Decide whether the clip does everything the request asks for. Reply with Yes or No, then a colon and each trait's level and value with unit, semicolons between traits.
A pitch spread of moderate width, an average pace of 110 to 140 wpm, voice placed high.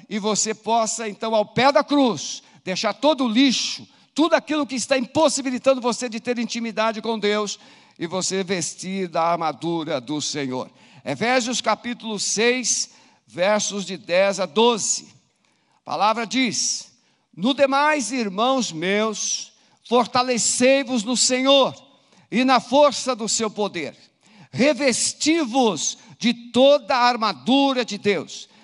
Yes: average, 3.9 semitones; average, 130 wpm; high, 235 Hz